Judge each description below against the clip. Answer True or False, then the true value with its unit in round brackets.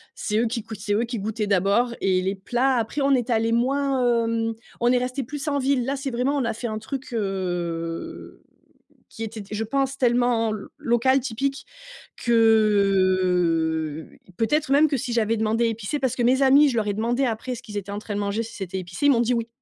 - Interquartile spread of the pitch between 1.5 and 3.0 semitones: False (3.7 semitones)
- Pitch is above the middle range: True (230 Hz)